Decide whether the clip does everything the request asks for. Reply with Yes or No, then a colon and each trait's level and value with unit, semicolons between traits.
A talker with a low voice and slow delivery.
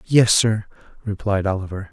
Yes: low, 105 Hz; slow, 125 wpm